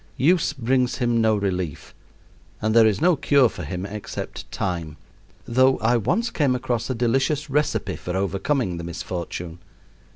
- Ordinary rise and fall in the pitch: No, wide, 6.1 semitones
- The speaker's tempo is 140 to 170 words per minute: Yes, average, 155 wpm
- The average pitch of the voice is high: No, low, 115 Hz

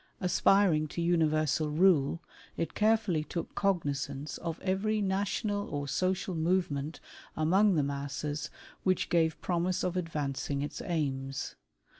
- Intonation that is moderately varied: Yes, average, 4.3 semitones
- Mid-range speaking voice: Yes, medium, 165 Hz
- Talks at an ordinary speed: No, slow, 120 wpm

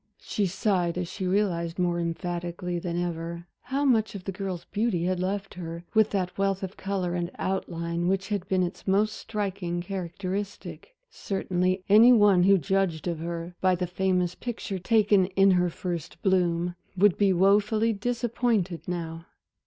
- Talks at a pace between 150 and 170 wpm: Yes, average, 160 wpm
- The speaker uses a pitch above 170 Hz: Yes, medium, 185 Hz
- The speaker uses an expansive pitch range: No, narrow, 2.5 semitones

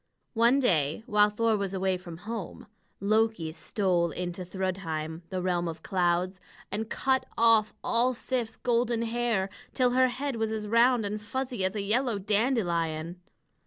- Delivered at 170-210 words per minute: No, average, 155 wpm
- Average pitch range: Yes, average, 4.4 semitones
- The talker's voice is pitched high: Yes, high, 210 Hz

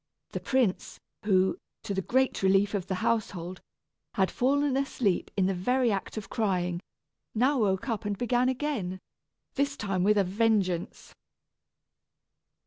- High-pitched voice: Yes, high, 205 Hz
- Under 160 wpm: Yes, average, 140 wpm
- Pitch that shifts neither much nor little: Yes, average, 4.9 semitones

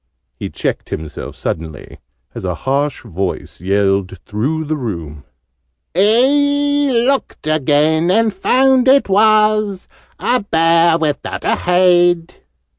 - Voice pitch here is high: No, medium, 170 Hz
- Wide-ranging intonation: Yes, wide, 8.9 semitones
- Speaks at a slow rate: Yes, slow, 115 wpm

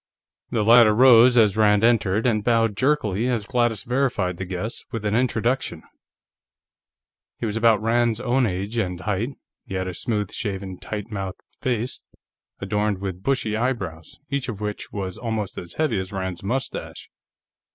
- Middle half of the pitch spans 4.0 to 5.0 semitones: No, average, 3.6 semitones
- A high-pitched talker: No, low, 110 Hz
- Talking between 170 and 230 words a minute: No, average, 160 wpm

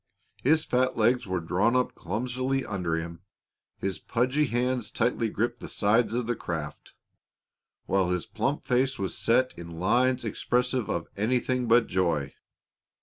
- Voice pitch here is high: No, low, 115 Hz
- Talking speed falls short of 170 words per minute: Yes, average, 145 wpm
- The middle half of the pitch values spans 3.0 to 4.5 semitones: No, average, 5.3 semitones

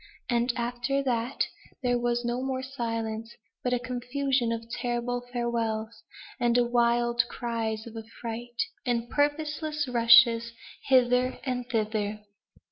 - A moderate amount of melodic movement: No, narrow, 1.4 semitones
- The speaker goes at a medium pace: No, slow, 120 wpm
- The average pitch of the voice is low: No, high, 240 Hz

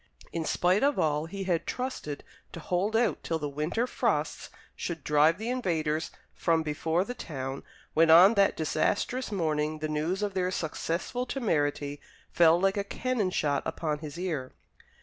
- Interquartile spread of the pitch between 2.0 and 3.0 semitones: No, average, 4.5 semitones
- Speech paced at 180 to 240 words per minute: No, average, 165 wpm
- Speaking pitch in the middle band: Yes, medium, 165 Hz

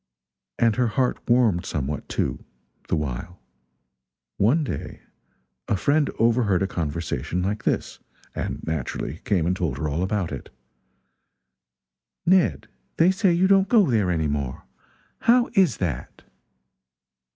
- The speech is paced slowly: Yes, slow, 130 wpm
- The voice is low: Yes, very low, 95 Hz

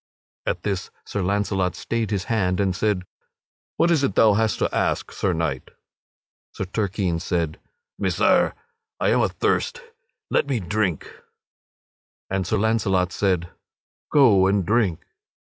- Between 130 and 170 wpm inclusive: Yes, slow, 135 wpm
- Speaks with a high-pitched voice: No, low, 100 Hz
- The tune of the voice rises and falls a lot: No, average, 3.2 semitones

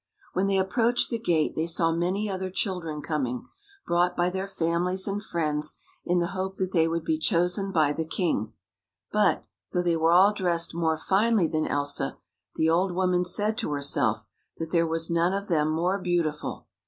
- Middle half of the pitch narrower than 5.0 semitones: Yes, average, 2.9 semitones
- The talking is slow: No, average, 185 wpm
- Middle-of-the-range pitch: Yes, medium, 175 Hz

